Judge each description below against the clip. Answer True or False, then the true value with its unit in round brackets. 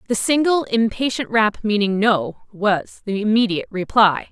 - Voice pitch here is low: False (215 Hz)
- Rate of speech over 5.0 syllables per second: False (4.6 syllables/s)